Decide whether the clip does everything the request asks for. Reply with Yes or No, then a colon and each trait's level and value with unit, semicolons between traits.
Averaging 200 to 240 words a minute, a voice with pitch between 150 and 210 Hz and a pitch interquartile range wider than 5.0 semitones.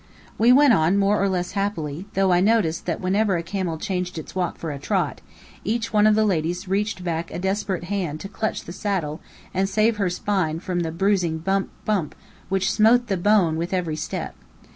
No: fast, 205 wpm; high, 190 Hz; average, 3.4 semitones